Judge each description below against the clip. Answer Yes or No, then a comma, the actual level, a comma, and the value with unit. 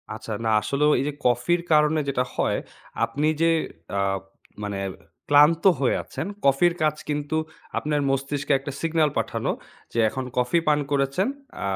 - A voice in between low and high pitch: Yes, medium, 145 Hz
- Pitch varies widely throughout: No, narrow, 2.6 semitones